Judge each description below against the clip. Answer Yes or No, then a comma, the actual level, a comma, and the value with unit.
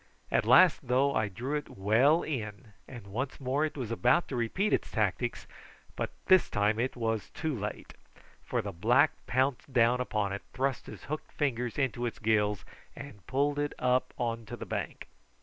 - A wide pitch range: No, average, 4.2 semitones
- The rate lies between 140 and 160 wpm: No, average, 185 wpm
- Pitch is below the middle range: Yes, low, 125 Hz